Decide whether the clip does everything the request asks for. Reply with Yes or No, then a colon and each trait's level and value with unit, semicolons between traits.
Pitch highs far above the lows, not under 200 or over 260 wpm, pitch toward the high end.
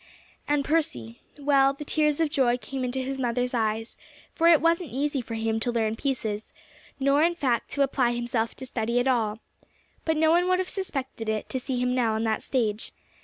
No: average, 4.2 semitones; fast, 205 wpm; very high, 255 Hz